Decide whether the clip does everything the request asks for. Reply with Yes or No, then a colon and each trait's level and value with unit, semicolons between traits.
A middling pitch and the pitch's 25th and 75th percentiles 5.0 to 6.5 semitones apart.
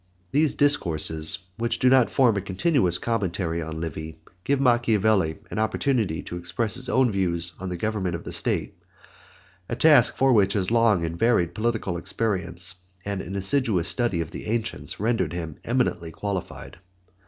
No: low, 100 Hz; wide, 5.4 semitones